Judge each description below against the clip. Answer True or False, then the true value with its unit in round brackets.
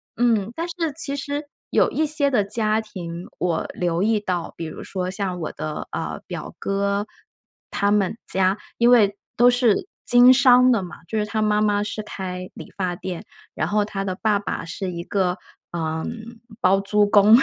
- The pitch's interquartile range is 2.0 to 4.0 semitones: True (3.6 semitones)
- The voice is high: True (205 Hz)